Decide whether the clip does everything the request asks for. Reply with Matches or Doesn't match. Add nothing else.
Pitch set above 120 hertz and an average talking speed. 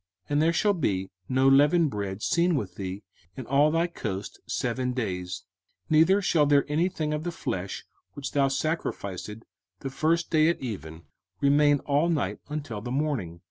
Matches